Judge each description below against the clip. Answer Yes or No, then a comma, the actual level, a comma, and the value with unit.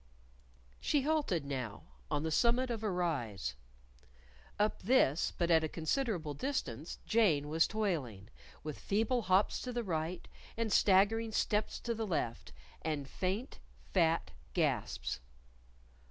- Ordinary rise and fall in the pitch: No, wide, 6.6 semitones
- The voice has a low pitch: No, medium, 185 Hz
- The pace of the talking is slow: Yes, slow, 130 wpm